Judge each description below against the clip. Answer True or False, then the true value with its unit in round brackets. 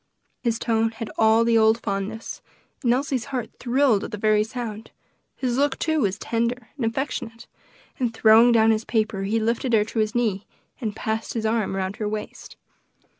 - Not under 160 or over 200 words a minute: True (180 wpm)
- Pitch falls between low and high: False (225 Hz)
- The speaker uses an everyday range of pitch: False (1.9 semitones)